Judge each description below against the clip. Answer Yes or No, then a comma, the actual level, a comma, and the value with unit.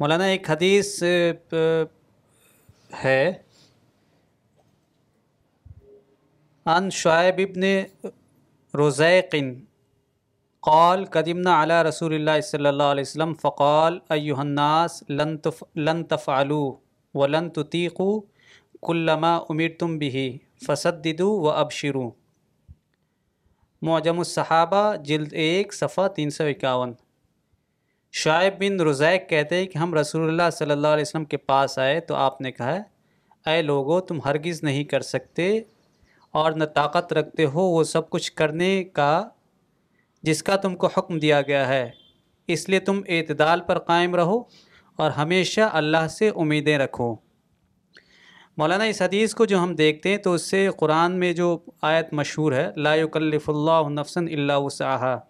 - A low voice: No, medium, 160 Hz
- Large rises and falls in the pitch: No, average, 3.3 semitones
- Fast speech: No, average, 135 wpm